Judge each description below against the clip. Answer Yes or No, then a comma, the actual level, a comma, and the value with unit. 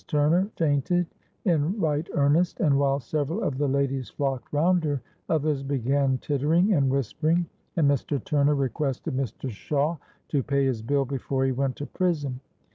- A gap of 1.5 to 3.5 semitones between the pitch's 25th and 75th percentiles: Yes, narrow, 2.4 semitones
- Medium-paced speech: Yes, average, 160 wpm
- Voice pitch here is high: No, medium, 145 Hz